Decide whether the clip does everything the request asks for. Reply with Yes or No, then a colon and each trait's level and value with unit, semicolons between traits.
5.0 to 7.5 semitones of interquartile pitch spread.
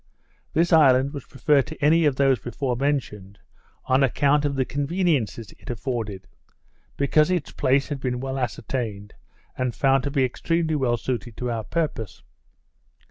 No: average, 3.3 semitones